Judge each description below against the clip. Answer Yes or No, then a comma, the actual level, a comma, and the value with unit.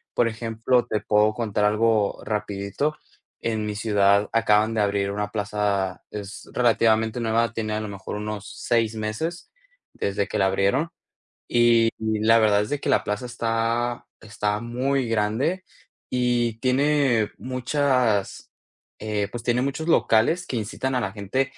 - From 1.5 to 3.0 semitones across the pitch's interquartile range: Yes, narrow, 2.6 semitones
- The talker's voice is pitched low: Yes, low, 110 Hz